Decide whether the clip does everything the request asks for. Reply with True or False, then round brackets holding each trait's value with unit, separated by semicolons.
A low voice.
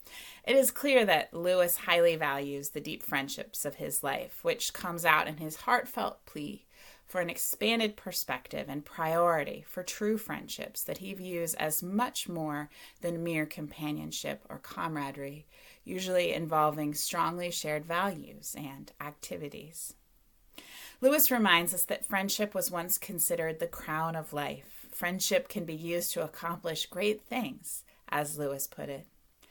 False (170 Hz)